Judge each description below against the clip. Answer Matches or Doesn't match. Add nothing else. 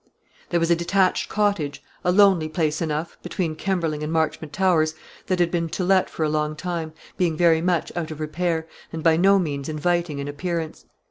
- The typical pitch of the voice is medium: Matches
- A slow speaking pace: Doesn't match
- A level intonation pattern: Matches